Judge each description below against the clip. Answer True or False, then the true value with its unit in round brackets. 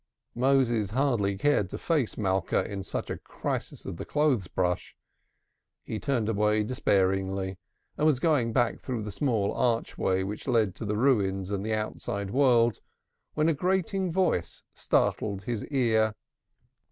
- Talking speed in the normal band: True (150 wpm)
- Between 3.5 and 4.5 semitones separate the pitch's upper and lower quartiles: False (5.1 semitones)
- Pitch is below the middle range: True (110 Hz)